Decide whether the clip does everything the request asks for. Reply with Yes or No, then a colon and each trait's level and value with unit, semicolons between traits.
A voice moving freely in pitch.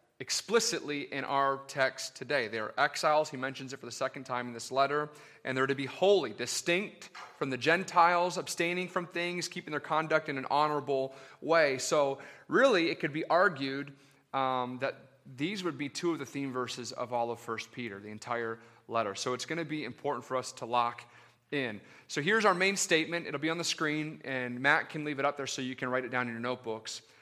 No: average, 4.0 semitones